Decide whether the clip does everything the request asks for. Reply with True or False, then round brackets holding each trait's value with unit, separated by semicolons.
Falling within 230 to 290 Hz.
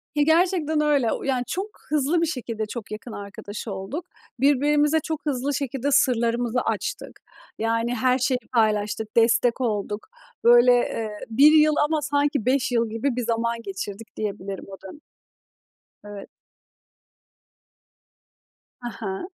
True (245 Hz)